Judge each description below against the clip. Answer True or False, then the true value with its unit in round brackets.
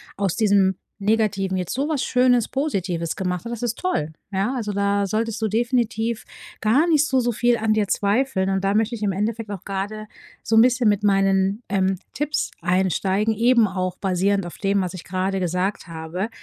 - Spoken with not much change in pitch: False (3.3 semitones)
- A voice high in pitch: True (205 Hz)